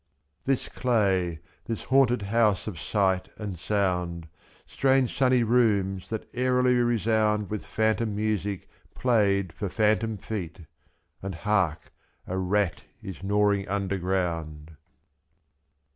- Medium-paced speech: No, slow, 115 wpm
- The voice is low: Yes, low, 105 Hz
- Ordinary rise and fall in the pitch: Yes, average, 3.2 semitones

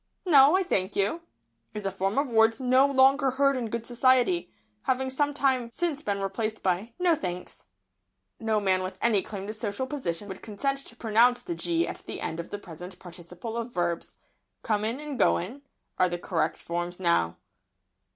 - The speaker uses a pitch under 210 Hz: No, high, 225 Hz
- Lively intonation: Yes, wide, 5.9 semitones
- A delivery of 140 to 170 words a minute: No, average, 185 wpm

